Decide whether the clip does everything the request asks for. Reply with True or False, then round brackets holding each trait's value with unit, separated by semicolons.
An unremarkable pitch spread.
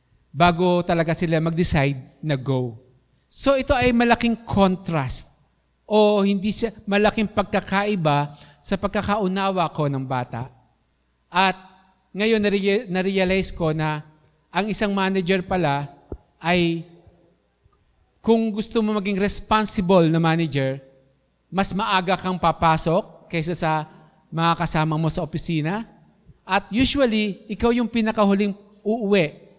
True (4.6 semitones)